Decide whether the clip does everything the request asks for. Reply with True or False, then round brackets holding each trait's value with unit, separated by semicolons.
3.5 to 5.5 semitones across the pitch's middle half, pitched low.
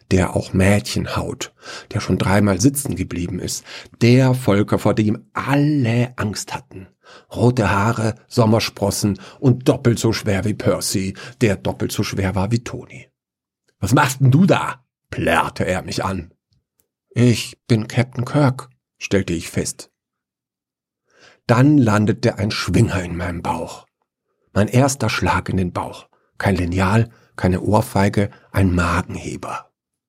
True (4.2 semitones; 105 Hz)